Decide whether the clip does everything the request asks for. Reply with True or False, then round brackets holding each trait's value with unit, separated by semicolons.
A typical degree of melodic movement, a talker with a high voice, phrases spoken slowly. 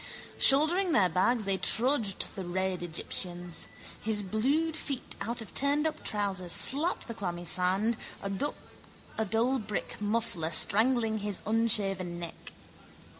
True (4.7 semitones; 210 Hz; 125 wpm)